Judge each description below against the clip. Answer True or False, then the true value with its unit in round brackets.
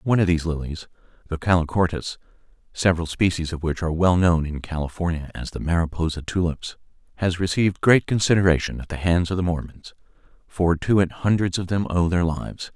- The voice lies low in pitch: True (85 Hz)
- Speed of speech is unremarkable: True (180 wpm)